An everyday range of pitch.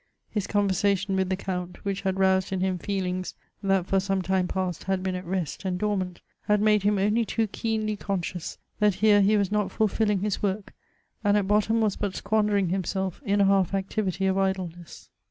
No: narrow, 1.8 semitones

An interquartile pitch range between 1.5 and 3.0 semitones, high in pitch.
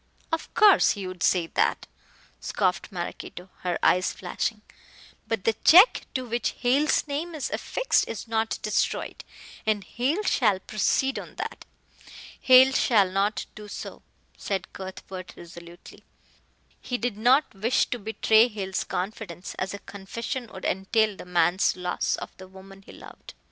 No: average, 4.5 semitones; high, 210 Hz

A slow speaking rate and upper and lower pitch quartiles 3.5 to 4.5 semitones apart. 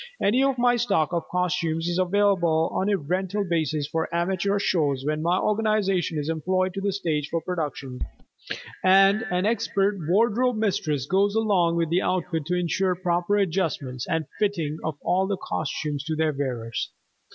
No: average, 165 wpm; average, 3.9 semitones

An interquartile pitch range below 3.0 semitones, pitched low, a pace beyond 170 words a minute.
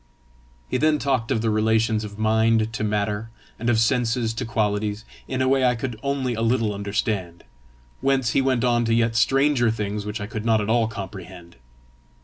Yes: narrow, 2.6 semitones; low, 115 Hz; average, 190 wpm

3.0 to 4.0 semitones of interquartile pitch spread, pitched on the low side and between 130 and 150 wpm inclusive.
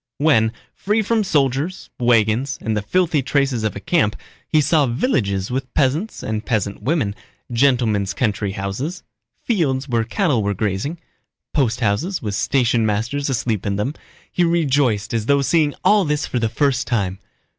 No: wide, 5.6 semitones; low, 125 Hz; average, 145 wpm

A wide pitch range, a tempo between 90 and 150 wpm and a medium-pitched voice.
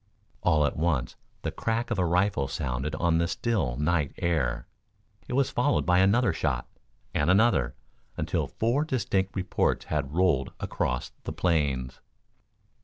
No: wide, 5.7 semitones; average, 145 wpm; very low, 85 Hz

